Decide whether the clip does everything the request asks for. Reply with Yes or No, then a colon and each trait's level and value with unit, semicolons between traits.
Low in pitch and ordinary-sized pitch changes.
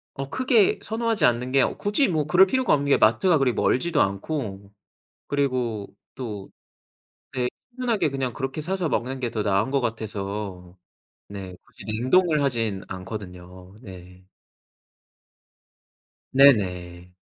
No: low, 125 Hz; wide, 7.1 semitones